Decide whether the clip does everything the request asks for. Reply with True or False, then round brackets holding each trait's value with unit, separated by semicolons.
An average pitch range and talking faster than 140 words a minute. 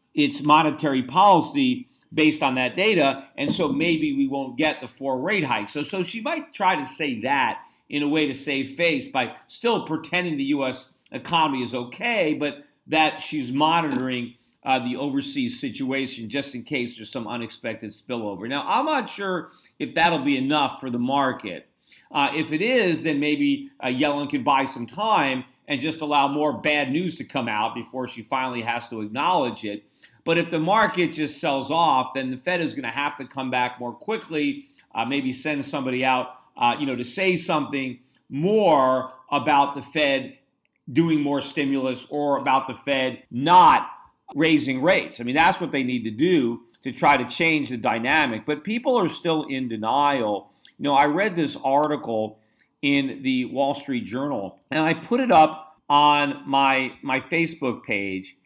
True (4.2 semitones; 185 wpm)